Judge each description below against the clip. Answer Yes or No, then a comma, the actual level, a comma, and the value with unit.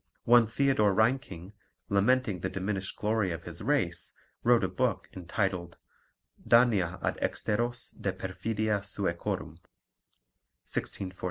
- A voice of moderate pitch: No, low, 100 Hz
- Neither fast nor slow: No, slow, 110 wpm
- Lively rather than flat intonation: No, average, 3.8 semitones